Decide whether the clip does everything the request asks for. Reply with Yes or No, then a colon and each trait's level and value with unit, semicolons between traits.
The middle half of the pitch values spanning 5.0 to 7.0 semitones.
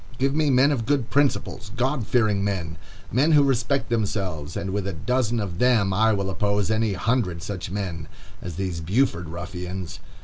Yes: wide, 5.6 semitones